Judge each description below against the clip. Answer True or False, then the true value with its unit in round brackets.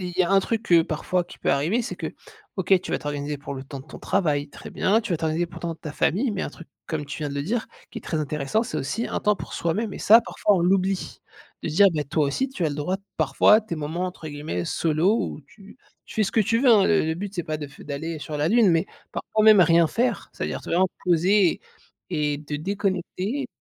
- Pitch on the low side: False (175 Hz)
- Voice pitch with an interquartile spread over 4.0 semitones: True (5.0 semitones)